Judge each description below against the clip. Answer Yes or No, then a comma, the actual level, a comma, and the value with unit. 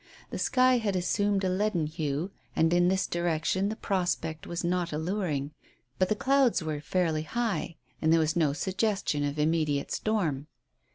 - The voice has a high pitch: No, medium, 175 Hz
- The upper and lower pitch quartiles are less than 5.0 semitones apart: Yes, average, 4.3 semitones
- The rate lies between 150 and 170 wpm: Yes, average, 165 wpm